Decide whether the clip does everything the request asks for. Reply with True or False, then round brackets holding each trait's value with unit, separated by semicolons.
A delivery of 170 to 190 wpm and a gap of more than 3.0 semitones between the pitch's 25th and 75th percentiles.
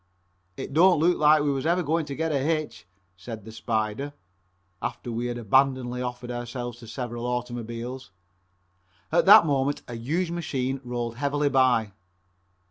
False (155 wpm; 3.5 semitones)